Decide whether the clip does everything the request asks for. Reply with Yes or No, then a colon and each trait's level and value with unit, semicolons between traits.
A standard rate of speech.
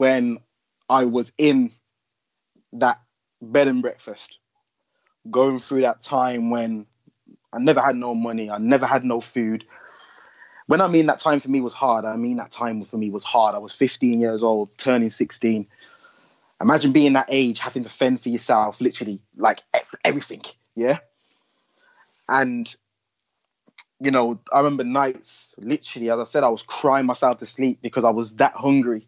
Yes: average, 165 wpm